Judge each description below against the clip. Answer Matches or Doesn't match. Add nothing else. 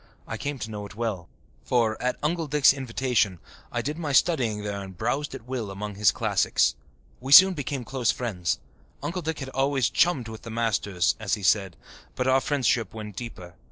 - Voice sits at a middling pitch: Doesn't match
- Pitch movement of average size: Matches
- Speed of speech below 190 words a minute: Doesn't match